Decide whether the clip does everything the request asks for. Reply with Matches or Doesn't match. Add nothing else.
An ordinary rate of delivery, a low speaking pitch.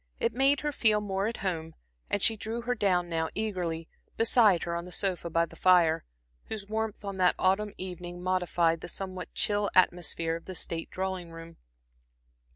Doesn't match